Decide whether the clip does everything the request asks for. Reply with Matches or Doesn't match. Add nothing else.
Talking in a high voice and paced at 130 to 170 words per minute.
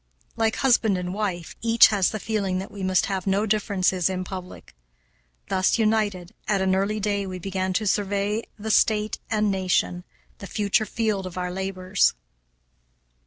Matches